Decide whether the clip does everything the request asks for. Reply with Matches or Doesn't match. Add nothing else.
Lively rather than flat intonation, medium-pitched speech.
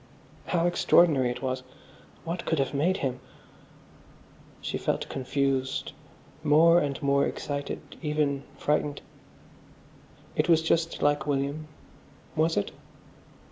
Doesn't match